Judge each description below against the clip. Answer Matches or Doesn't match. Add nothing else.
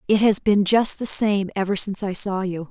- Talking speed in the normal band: Doesn't match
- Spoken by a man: Doesn't match